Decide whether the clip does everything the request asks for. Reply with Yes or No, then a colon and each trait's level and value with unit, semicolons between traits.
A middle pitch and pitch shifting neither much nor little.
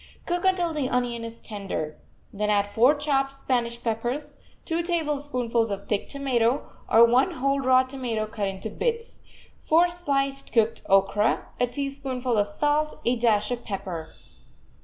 No: high, 245 Hz; average, 4.2 semitones